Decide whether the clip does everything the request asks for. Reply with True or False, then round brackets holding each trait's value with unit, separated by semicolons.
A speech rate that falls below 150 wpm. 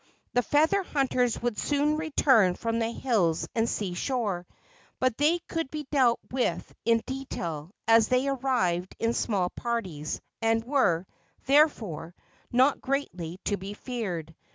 True (140 wpm)